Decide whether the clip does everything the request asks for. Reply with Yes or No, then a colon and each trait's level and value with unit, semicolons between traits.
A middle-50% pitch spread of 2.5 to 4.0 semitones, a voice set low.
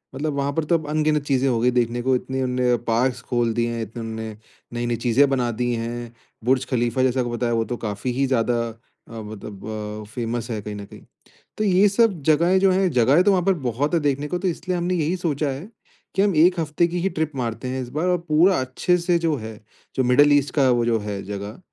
No: average, 5.2 semitones; low, 130 Hz